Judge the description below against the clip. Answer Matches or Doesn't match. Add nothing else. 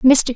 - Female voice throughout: Matches